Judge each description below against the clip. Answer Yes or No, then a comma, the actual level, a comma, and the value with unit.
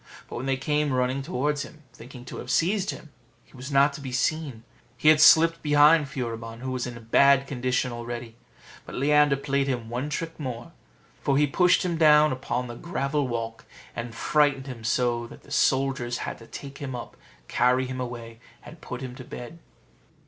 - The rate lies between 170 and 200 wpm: Yes, average, 195 wpm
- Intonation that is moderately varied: Yes, average, 3.3 semitones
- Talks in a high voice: No, low, 135 Hz